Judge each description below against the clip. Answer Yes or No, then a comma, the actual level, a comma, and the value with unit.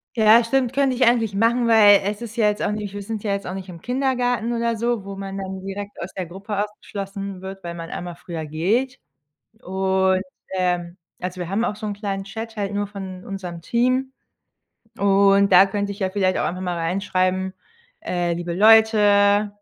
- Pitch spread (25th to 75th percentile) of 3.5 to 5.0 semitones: No, average, 2.8 semitones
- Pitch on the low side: No, high, 200 Hz